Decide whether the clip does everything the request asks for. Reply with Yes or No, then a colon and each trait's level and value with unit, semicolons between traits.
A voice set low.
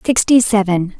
No: high, 210 Hz